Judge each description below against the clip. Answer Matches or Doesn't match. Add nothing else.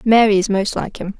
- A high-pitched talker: Matches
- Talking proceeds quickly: Matches